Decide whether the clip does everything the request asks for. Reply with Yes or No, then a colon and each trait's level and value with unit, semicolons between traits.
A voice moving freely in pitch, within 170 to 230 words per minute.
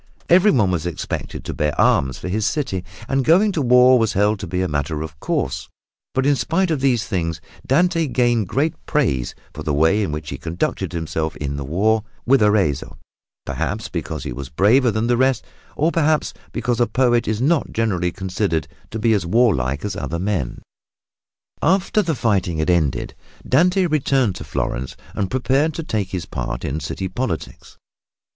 Yes: wide, 8.1 semitones; average, 180 wpm